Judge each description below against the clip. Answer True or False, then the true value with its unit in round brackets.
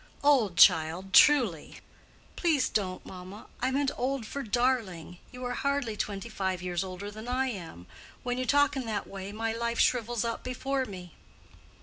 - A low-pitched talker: False (225 Hz)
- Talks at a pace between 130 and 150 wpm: False (165 wpm)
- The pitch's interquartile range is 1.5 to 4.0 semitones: False (5.2 semitones)